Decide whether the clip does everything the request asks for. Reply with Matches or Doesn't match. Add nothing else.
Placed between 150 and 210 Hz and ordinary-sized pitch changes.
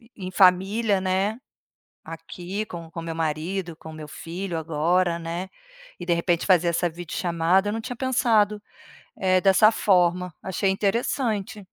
Matches